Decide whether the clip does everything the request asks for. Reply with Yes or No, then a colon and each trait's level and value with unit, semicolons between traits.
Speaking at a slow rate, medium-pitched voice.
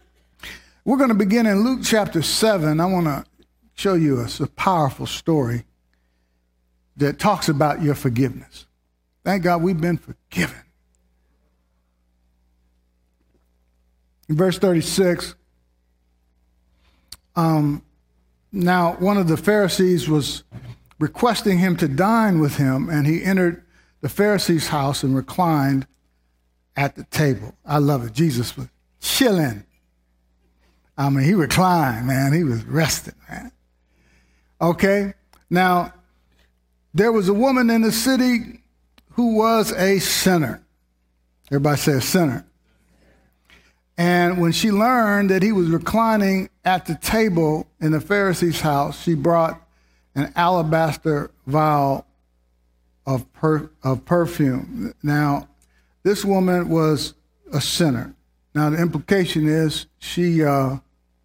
Yes: slow, 120 wpm; medium, 145 Hz